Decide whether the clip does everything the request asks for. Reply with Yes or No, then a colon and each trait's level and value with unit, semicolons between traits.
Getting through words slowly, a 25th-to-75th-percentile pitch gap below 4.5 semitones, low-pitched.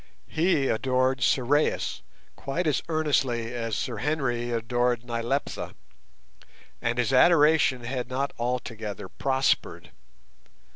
Yes: slow, 100 wpm; average, 2.8 semitones; low, 125 Hz